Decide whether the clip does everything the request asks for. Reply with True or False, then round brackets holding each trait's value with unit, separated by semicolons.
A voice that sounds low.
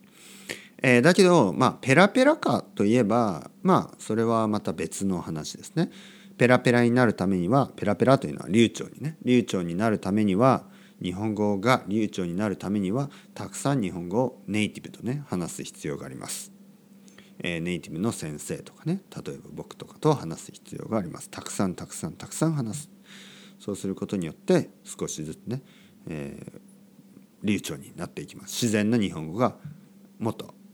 True (125 Hz)